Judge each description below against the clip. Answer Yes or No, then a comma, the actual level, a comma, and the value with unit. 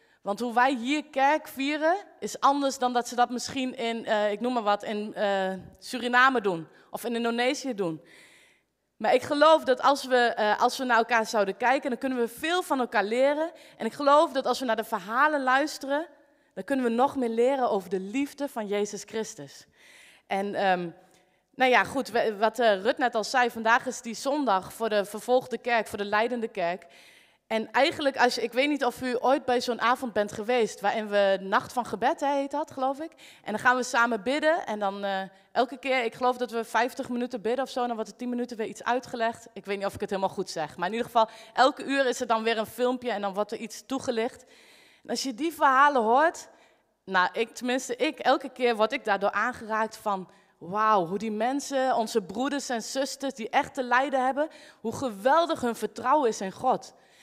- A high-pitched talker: Yes, high, 240 Hz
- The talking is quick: Yes, fast, 220 wpm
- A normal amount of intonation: Yes, average, 3.5 semitones